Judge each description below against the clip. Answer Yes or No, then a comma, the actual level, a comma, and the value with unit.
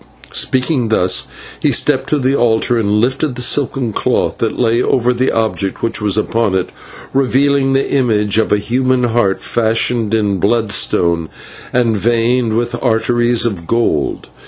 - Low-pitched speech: Yes, low, 115 Hz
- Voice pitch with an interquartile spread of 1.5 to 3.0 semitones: Yes, average, 2.7 semitones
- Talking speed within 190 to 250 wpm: No, average, 155 wpm